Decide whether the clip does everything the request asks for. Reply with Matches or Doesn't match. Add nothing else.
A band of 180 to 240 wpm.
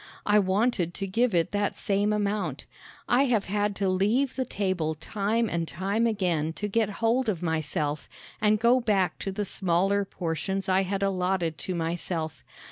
Doesn't match